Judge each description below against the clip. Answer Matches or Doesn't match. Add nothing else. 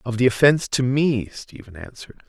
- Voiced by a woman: Doesn't match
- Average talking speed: Matches